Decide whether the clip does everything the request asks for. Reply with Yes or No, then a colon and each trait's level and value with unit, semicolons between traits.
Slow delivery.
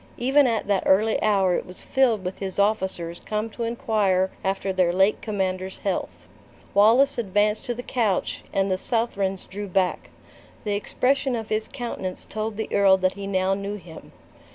No: average, 175 wpm